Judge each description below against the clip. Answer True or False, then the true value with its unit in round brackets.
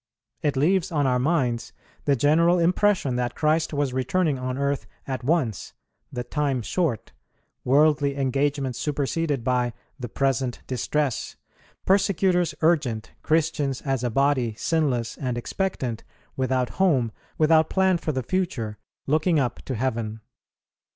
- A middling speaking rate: False (130 wpm)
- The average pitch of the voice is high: False (140 Hz)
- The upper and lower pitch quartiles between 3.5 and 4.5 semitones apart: True (4.2 semitones)